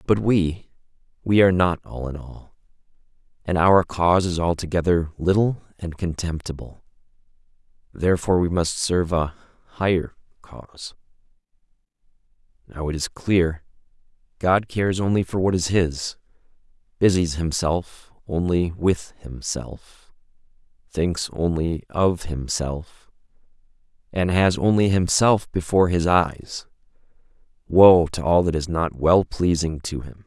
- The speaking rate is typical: No, slow, 115 wpm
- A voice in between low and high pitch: No, very low, 85 Hz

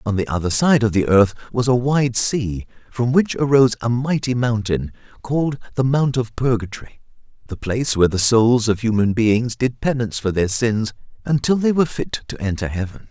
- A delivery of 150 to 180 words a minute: No, average, 190 wpm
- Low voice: Yes, low, 120 Hz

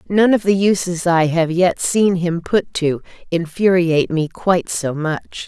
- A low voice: No, medium, 175 Hz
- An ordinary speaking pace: Yes, average, 175 wpm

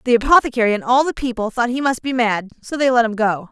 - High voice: Yes, high, 240 Hz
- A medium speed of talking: No, fast, 275 wpm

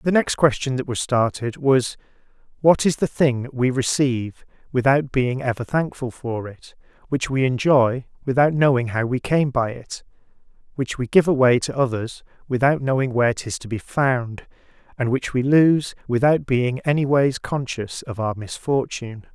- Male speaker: Yes, male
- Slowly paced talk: No, average, 165 wpm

